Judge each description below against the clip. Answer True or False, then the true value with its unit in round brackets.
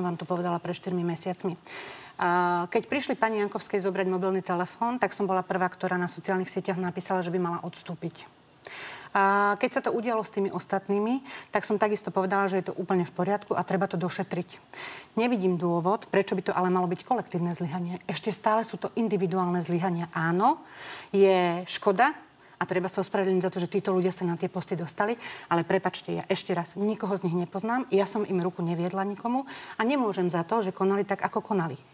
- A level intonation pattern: True (2.2 semitones)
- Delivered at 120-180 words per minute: False (195 wpm)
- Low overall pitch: False (190 Hz)